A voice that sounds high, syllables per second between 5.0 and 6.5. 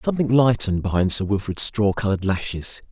No: low, 105 Hz; 6.2 syllables/s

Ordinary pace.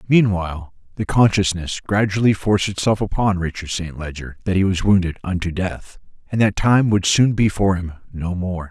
Yes: average, 180 wpm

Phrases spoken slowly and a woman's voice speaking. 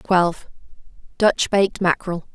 Yes: slow, 75 wpm; female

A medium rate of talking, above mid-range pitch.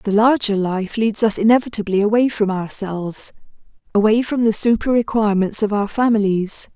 Yes: average, 150 wpm; high, 215 Hz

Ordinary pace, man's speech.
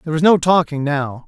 No: fast, 235 wpm; male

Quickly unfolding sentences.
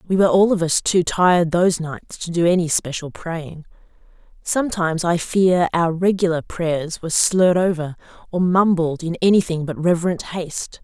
No: average, 165 wpm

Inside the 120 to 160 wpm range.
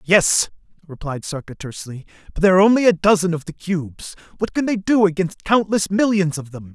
No: average, 195 wpm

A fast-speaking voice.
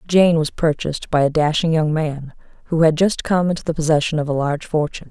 Yes: fast, 225 wpm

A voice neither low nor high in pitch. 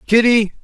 No: high, 220 Hz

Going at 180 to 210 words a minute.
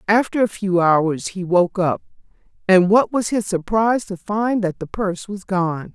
Yes: average, 190 wpm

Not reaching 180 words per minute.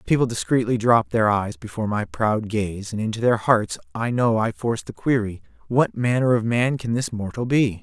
No: fast, 205 wpm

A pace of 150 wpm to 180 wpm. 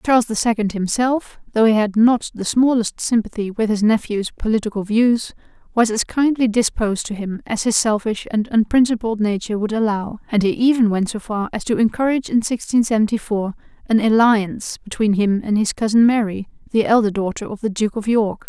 No: average, 190 wpm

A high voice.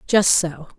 No: medium, 170 Hz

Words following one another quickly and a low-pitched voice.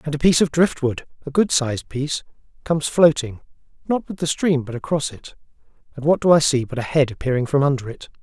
No: fast, 220 wpm; medium, 145 Hz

